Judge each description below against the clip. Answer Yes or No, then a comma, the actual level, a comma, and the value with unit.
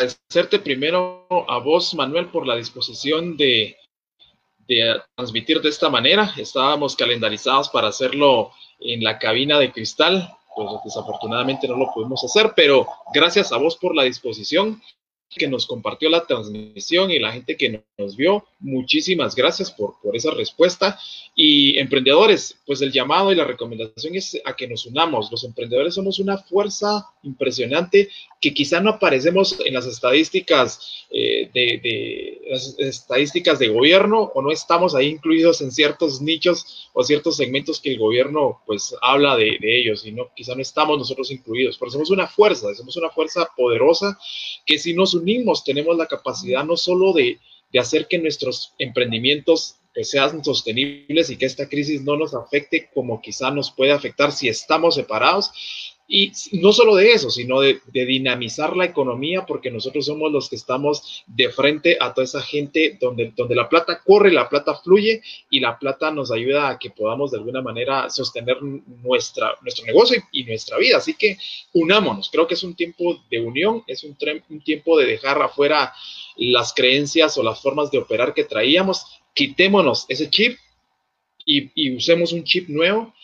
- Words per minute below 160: No, average, 175 wpm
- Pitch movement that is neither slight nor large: No, wide, 7.9 semitones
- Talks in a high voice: No, medium, 165 Hz